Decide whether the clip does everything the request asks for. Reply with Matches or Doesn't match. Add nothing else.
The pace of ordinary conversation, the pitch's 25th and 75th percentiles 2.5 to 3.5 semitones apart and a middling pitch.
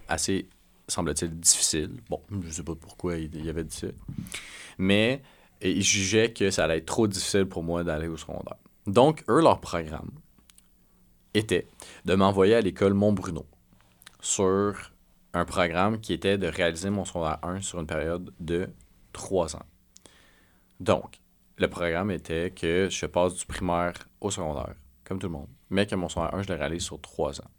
Doesn't match